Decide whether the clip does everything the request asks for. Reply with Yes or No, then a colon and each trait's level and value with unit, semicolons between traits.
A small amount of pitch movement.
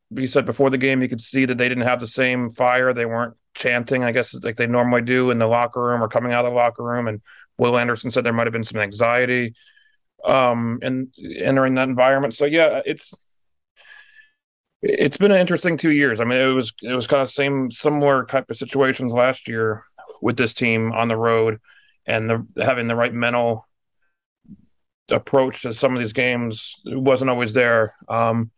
Yes: narrow, 2.2 semitones